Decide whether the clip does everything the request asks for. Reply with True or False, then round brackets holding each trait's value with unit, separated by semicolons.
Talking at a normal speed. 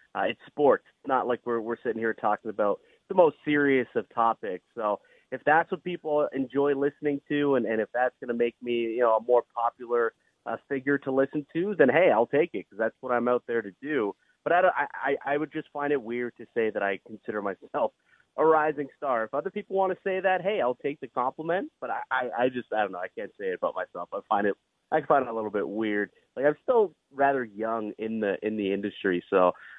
False (245 wpm)